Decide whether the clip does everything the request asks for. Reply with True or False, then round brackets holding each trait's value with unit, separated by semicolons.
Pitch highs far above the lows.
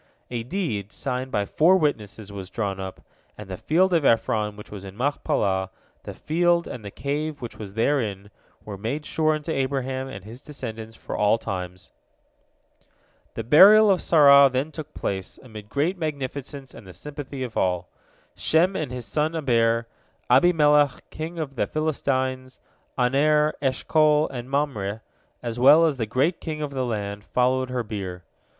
True (5.8 semitones)